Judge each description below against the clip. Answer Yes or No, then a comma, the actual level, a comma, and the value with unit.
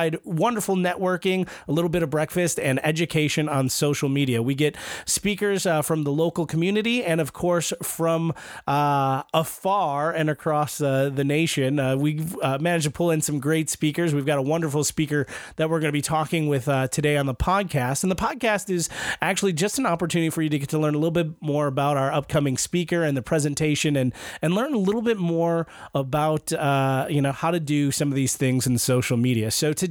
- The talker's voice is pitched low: No, medium, 155 Hz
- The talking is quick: Yes, fast, 215 wpm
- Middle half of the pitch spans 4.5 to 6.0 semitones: No, average, 3.1 semitones